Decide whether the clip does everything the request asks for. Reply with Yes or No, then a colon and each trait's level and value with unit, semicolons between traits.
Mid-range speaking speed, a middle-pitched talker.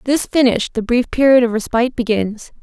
No: average, 185 wpm; high, 240 Hz